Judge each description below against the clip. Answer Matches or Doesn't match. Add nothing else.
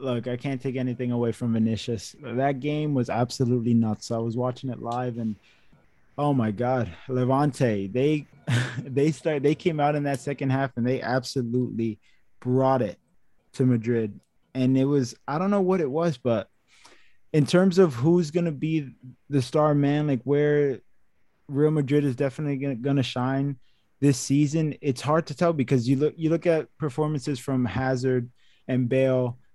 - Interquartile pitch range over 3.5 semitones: Doesn't match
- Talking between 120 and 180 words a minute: Matches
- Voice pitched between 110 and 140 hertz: Matches